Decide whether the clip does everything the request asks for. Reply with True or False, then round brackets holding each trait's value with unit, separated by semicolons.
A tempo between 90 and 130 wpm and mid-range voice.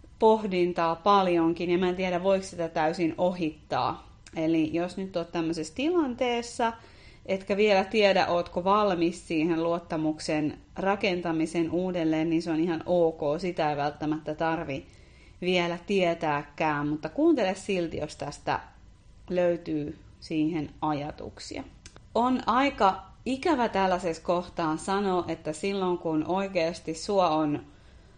True (120 wpm; 175 Hz)